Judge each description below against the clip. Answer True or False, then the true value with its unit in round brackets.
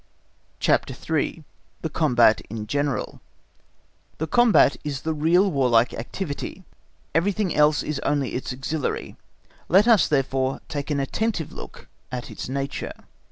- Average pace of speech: False (130 wpm)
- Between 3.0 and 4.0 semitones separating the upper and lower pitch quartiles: True (3.6 semitones)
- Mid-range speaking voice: True (145 Hz)